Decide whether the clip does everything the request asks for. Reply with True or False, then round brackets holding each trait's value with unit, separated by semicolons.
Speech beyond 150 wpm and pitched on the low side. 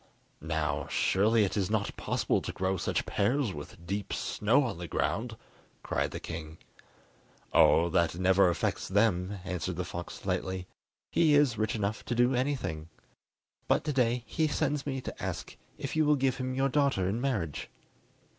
True (170 wpm; 105 Hz)